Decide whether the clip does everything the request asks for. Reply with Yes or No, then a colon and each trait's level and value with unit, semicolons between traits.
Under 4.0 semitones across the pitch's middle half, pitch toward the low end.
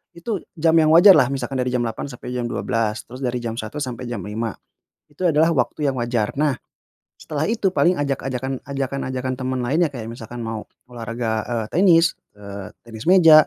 No: average, 4.7 semitones; low, 130 Hz